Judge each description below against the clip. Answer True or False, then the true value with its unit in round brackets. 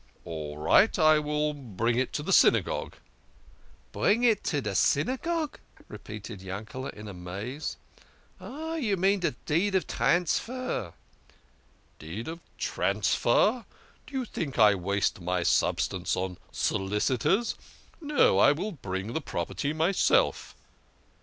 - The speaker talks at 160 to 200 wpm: False (145 wpm)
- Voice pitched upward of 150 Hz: False (145 Hz)